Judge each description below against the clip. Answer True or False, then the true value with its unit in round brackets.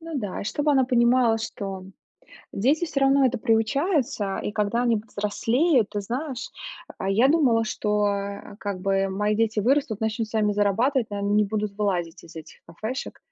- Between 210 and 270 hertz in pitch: True (220 Hz)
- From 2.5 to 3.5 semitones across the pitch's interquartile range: False (4.1 semitones)